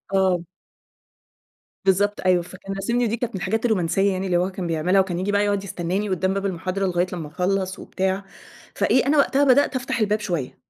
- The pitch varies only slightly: Yes, narrow, 2.2 semitones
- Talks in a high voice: Yes, high, 195 Hz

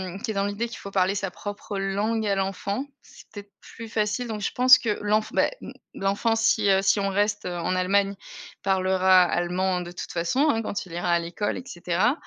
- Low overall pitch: No, high, 200 Hz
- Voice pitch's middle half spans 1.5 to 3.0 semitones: Yes, narrow, 2.4 semitones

